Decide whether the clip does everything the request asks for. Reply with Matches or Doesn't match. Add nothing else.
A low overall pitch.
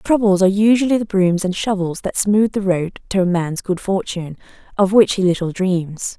Doesn't match